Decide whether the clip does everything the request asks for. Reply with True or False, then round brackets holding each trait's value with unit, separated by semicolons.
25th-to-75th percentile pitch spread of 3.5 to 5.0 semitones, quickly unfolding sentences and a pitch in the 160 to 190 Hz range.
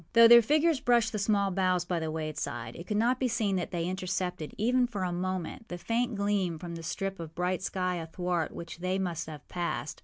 True (4.0 semitones; 220 wpm; 185 Hz)